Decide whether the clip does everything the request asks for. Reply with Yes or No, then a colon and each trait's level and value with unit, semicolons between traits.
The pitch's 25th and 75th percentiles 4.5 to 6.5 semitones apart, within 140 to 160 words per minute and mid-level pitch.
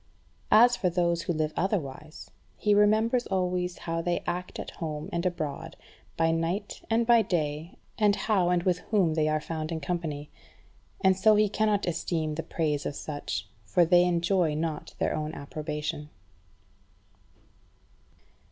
No: average, 3.6 semitones; average, 150 wpm; medium, 170 Hz